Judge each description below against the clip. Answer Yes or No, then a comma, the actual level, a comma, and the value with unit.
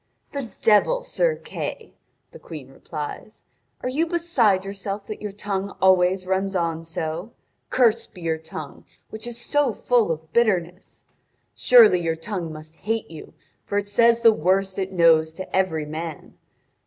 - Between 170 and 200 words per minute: No, average, 155 wpm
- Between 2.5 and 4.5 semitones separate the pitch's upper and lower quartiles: No, wide, 5.5 semitones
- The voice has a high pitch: Yes, high, 195 Hz